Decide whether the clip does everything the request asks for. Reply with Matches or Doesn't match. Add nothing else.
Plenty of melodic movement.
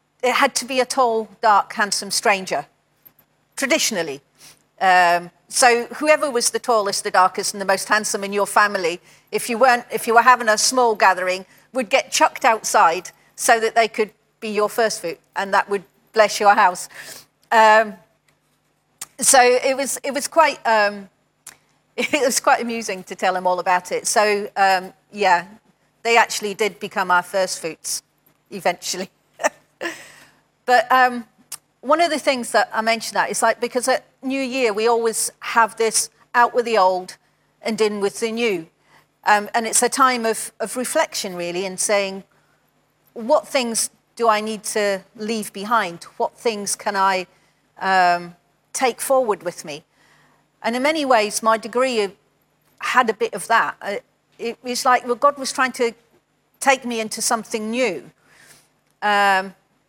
Doesn't match